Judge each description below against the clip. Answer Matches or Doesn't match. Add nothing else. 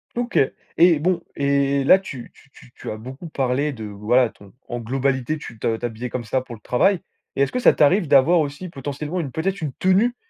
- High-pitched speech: Doesn't match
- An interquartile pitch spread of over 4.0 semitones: Matches